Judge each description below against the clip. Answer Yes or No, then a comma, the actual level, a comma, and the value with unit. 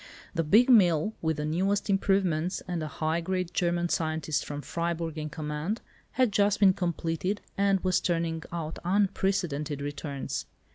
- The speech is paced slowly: No, average, 150 wpm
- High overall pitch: No, medium, 170 Hz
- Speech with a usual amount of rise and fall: Yes, average, 3.6 semitones